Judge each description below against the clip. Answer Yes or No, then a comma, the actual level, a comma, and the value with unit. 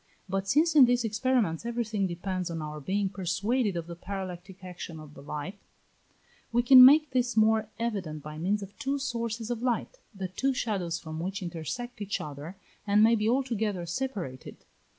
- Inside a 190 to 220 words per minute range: No, average, 175 wpm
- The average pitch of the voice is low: No, high, 200 Hz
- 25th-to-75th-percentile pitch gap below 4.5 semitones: No, wide, 5.5 semitones